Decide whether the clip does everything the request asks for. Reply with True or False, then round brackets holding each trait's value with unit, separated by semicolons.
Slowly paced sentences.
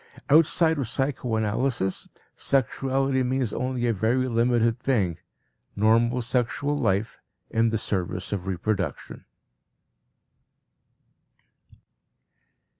True (85 wpm)